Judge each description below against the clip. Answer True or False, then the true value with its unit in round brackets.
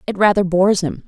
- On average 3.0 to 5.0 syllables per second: False (6.5 syllables/s)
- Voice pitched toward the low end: False (185 Hz)